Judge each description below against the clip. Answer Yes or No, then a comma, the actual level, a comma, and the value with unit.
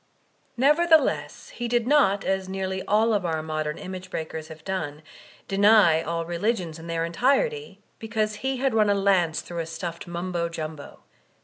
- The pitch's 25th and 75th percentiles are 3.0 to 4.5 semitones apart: No, average, 5.0 semitones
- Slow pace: No, average, 170 wpm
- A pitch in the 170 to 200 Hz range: Yes, high, 190 Hz